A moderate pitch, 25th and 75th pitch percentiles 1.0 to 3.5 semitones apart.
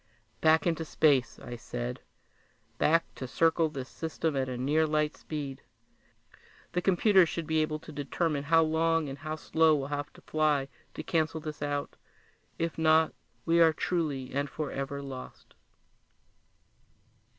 Yes: medium, 155 Hz; narrow, 2.4 semitones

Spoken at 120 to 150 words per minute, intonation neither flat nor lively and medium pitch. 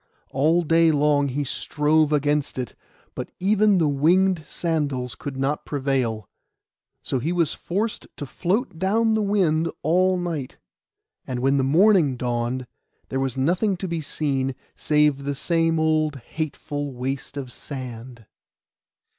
Yes: average, 140 wpm; average, 4.2 semitones; medium, 150 Hz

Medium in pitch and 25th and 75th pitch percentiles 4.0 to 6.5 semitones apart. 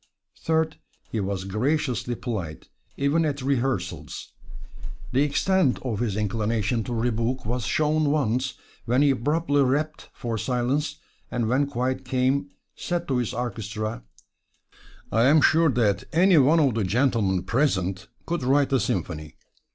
No: low, 125 Hz; average, 4.5 semitones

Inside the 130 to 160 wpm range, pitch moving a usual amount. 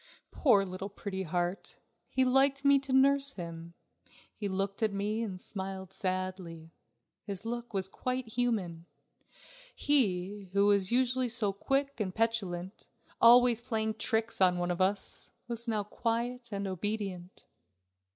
Yes: average, 140 wpm; average, 4.3 semitones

